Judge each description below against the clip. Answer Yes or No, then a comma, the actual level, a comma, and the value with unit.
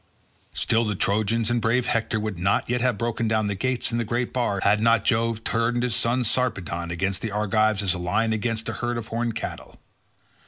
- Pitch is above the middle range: No, low, 115 Hz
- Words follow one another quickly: Yes, fast, 210 wpm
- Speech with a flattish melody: Yes, narrow, 2.2 semitones